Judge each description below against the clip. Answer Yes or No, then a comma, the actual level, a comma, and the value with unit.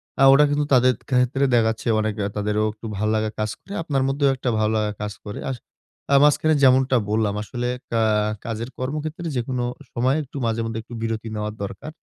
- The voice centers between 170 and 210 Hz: No, low, 120 Hz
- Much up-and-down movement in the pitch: No, average, 3.8 semitones